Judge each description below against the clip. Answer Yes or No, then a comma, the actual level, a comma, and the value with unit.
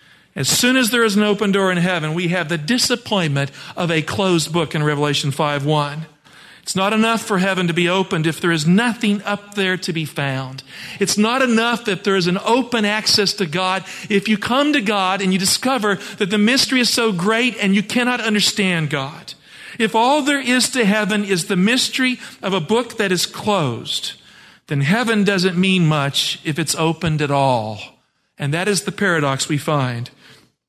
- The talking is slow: No, average, 195 wpm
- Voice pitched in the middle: No, high, 195 Hz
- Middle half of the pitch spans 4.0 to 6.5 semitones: Yes, average, 5.0 semitones